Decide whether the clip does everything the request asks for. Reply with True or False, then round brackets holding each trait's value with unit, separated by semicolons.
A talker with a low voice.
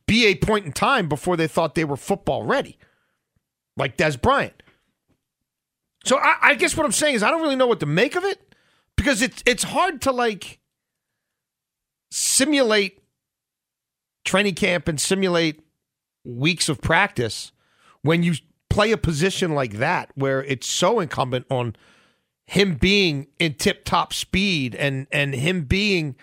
False (175 Hz)